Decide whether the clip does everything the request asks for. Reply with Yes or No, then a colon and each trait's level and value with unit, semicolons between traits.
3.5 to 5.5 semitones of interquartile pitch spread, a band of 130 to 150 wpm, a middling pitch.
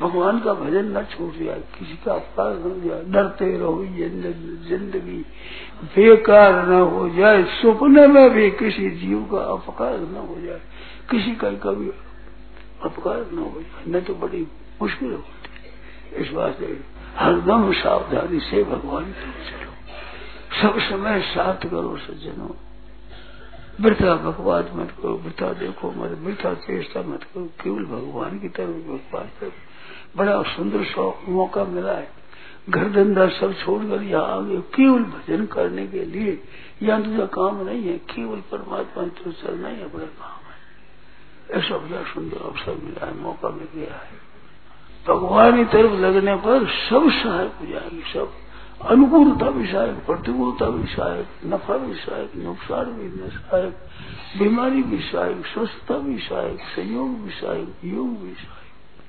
No: average, 4.4 semitones; average, 135 wpm; high, 200 Hz